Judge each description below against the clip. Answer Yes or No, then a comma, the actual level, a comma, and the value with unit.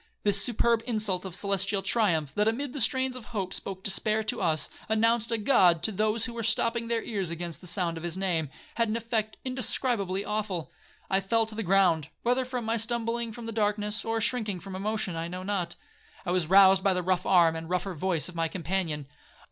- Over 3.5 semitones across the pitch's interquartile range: Yes, average, 3.9 semitones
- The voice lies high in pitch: Yes, high, 200 Hz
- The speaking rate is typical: No, fast, 210 wpm